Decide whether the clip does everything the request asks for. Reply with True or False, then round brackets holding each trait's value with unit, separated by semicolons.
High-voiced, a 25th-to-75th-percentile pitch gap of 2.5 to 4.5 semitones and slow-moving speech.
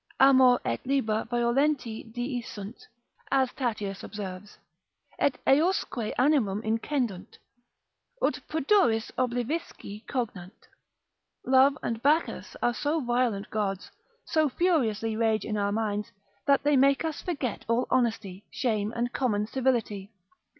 True (240 Hz; 4.2 semitones; 120 wpm)